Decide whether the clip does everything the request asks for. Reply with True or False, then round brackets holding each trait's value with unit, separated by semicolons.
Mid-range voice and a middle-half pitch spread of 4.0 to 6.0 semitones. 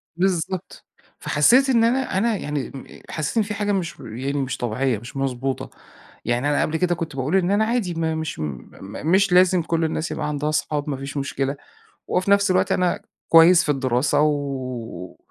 True (155 Hz; 5.3 semitones)